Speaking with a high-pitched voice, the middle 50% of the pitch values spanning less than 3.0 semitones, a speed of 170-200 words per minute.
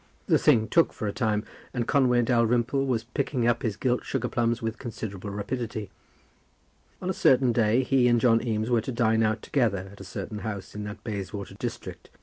No: low, 115 Hz; narrow, 2.4 semitones; average, 195 wpm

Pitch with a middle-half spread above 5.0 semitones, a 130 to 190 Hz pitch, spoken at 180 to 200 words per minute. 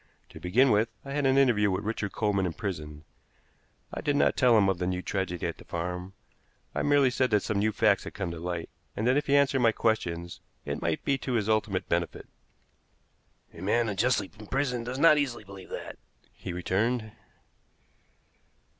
No: wide, 5.5 semitones; low, 105 Hz; average, 190 wpm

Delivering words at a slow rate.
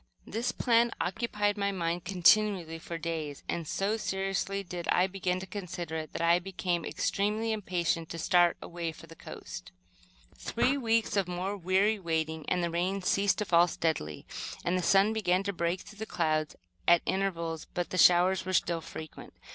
No: average, 180 wpm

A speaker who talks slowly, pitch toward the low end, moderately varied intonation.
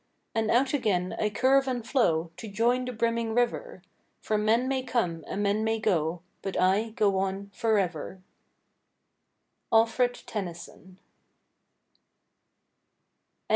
No: slow, 120 wpm; high, 215 Hz; average, 3.9 semitones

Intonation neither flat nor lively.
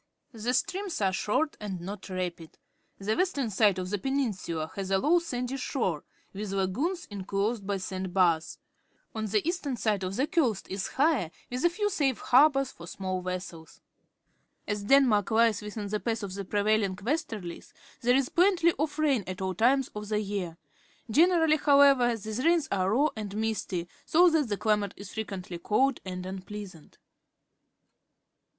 No: wide, 6.2 semitones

